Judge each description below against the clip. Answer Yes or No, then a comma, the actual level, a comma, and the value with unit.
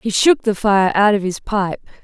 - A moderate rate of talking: No, fast, 235 wpm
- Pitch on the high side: Yes, high, 205 Hz